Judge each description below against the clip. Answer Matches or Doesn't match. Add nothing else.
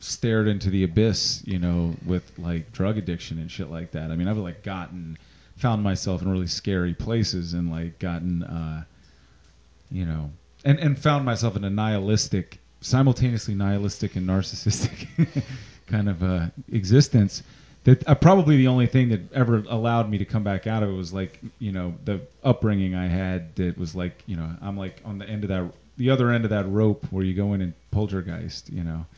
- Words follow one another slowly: Doesn't match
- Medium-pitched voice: Doesn't match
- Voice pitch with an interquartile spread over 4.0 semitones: Matches